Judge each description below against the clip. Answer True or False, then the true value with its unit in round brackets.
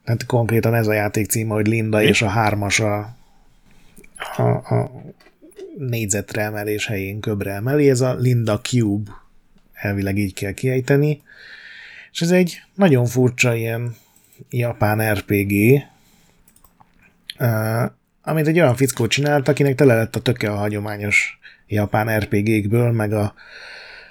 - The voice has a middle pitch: False (110 Hz)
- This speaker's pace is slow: False (125 wpm)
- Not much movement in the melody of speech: False (3.7 semitones)